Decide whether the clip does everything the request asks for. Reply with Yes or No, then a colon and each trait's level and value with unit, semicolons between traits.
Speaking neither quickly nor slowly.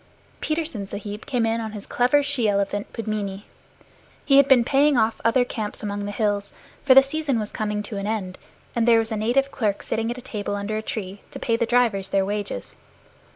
No: fast, 210 wpm